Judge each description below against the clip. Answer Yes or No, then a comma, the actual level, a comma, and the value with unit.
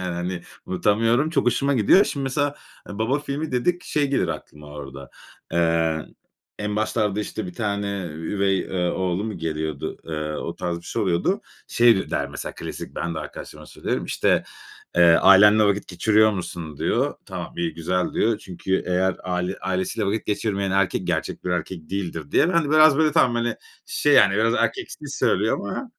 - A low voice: Yes, very low, 95 Hz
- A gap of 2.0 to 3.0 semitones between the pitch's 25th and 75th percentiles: No, average, 4.8 semitones